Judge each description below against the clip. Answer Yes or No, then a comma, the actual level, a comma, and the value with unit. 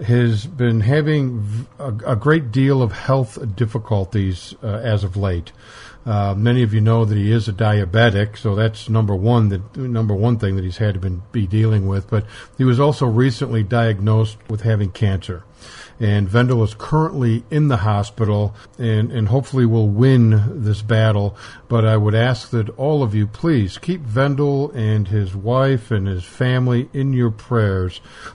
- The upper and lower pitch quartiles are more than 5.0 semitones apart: No, average, 2.8 semitones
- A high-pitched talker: No, low, 110 Hz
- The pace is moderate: Yes, average, 180 wpm